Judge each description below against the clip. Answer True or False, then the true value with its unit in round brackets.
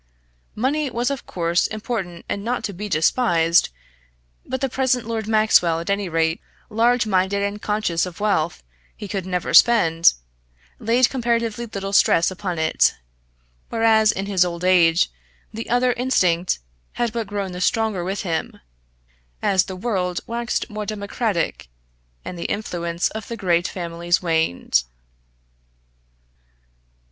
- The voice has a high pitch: True (200 Hz)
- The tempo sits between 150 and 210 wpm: False (140 wpm)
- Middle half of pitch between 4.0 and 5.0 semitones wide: True (4.7 semitones)